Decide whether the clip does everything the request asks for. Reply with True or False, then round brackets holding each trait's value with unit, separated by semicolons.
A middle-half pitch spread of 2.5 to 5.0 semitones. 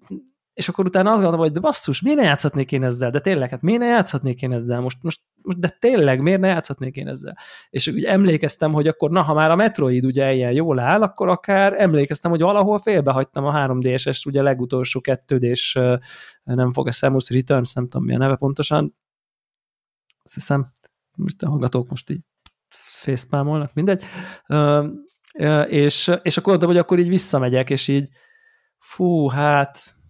False (5.6 semitones)